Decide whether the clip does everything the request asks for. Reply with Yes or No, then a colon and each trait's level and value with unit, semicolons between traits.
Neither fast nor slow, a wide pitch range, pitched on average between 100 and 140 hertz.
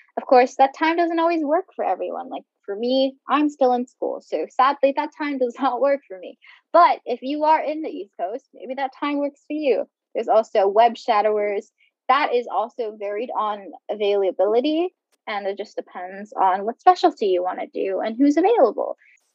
No: average, 195 wpm; wide, 6.2 semitones; very high, 260 Hz